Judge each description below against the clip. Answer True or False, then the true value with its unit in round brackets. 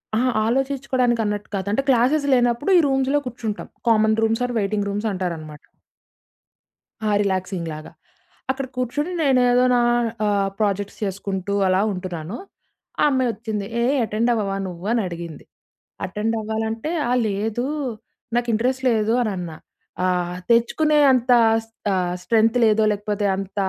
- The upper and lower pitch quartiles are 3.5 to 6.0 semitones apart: True (3.9 semitones)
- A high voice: True (220 Hz)